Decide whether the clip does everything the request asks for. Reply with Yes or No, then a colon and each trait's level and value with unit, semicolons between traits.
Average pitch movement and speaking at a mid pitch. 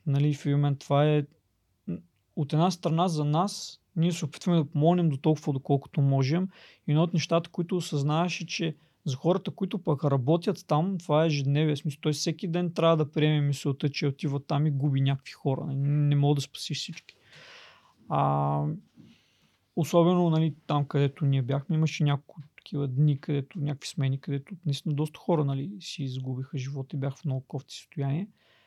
Yes: average, 3.0 semitones; medium, 150 Hz